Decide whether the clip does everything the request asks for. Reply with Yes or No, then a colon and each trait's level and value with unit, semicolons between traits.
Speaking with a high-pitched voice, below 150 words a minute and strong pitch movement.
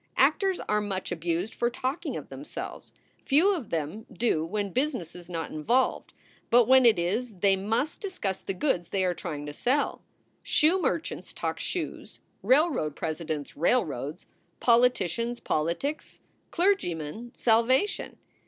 Yes: high, 210 Hz; average, 140 wpm; wide, 7.3 semitones